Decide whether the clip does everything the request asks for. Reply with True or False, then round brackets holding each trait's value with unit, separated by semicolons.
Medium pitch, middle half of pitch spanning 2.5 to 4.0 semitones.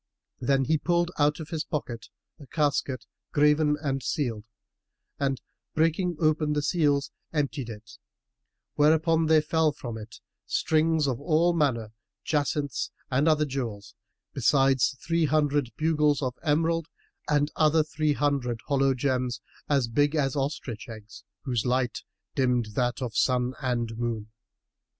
True (145 Hz; 3.6 semitones)